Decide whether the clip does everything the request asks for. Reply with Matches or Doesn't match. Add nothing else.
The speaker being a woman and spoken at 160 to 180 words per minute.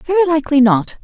Matches